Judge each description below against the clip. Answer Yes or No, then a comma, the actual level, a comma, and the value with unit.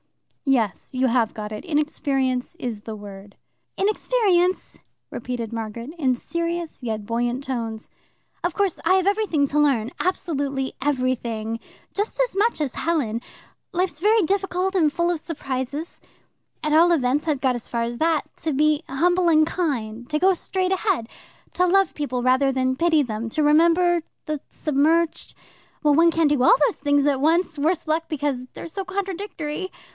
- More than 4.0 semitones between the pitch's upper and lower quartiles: Yes, wide, 5.4 semitones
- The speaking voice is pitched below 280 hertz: No, very high, 295 Hz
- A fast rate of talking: No, average, 165 wpm